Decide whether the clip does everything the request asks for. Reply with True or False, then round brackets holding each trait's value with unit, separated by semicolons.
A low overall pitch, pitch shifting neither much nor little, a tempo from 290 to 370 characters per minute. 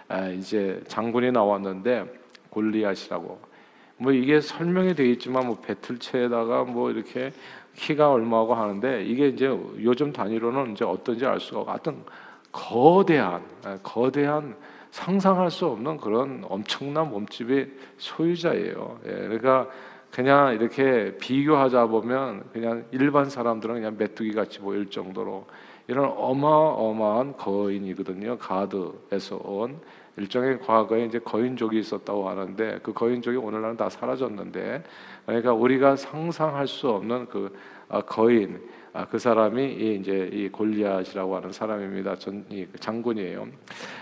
True (120 Hz; 4.0 semitones; 300 characters per minute)